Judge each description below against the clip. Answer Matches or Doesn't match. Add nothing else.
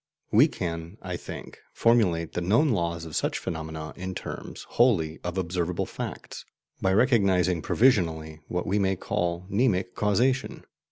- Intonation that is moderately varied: Matches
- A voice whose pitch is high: Doesn't match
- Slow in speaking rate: Doesn't match